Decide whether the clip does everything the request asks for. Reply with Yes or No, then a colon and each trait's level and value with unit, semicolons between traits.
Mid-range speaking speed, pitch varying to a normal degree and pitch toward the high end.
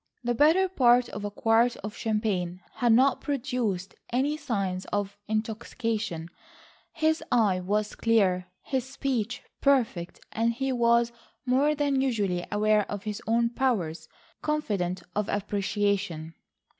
No: slow, 130 wpm; average, 4.2 semitones; high, 225 Hz